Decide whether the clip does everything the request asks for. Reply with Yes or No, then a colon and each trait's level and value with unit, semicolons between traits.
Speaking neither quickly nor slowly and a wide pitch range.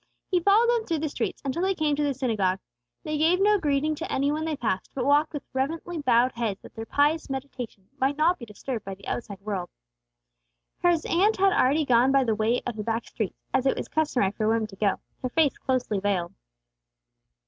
No: fast, 215 wpm; wide, 5.8 semitones